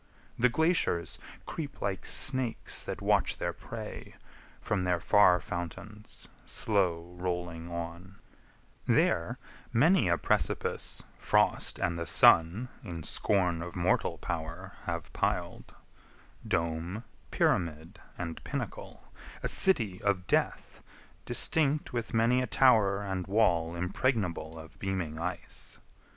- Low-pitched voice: Yes, very low, 90 Hz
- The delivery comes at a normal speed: No, slow, 115 wpm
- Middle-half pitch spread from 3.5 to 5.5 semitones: Yes, average, 4.4 semitones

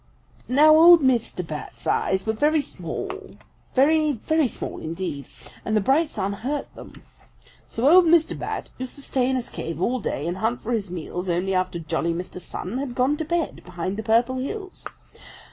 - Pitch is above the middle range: Yes, high, 240 Hz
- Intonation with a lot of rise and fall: Yes, wide, 8.2 semitones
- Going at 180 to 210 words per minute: Yes, average, 185 wpm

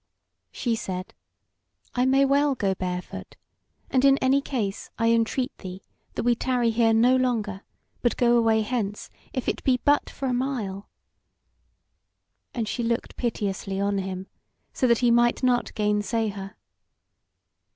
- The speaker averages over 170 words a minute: No, average, 150 wpm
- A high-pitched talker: Yes, high, 230 Hz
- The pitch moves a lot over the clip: No, average, 3.8 semitones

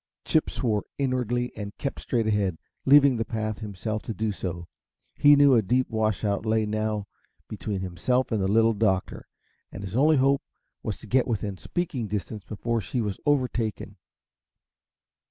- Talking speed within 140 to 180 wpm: Yes, average, 160 wpm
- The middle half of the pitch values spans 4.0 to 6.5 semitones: No, average, 3.6 semitones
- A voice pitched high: No, low, 110 Hz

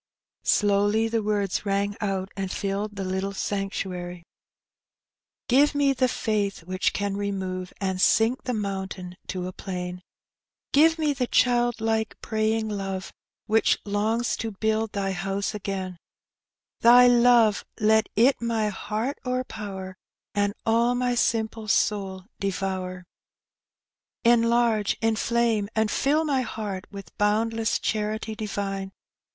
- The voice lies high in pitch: Yes, high, 210 Hz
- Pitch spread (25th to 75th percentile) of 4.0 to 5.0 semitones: No, average, 2.8 semitones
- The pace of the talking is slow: Yes, slow, 130 wpm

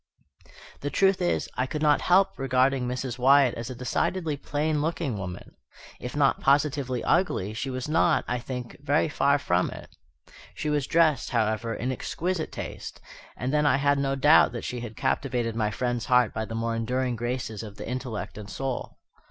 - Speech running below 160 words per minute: No, average, 185 wpm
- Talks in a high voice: No, low, 130 Hz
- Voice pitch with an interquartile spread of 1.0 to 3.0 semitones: No, average, 3.5 semitones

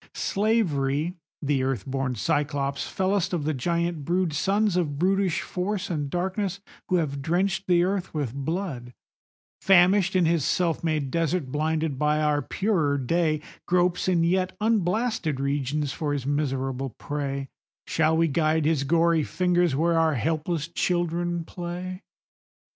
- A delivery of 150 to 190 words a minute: No, average, 140 wpm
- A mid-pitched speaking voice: Yes, medium, 165 Hz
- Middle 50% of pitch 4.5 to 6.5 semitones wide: No, average, 3.8 semitones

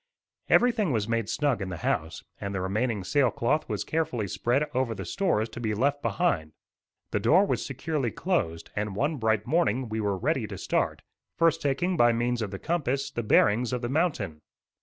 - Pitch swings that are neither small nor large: No, wide, 6.1 semitones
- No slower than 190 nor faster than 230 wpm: Yes, average, 195 wpm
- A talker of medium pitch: No, low, 120 Hz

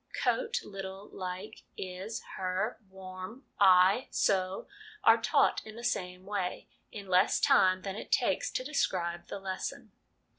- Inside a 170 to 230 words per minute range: No, average, 145 wpm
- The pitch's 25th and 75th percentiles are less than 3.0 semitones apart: Yes, narrow, 2.4 semitones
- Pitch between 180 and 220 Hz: Yes, high, 190 Hz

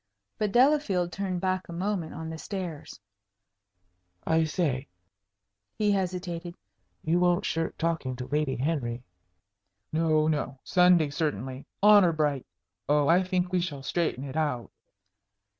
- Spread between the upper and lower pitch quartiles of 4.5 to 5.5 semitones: No, average, 3.7 semitones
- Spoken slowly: Yes, slow, 130 wpm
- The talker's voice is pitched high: No, medium, 165 Hz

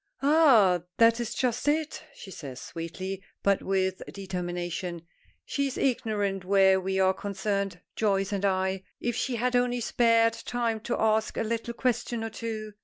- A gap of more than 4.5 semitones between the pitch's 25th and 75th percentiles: No, average, 3.8 semitones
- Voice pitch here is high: Yes, high, 210 Hz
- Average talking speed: Yes, average, 160 wpm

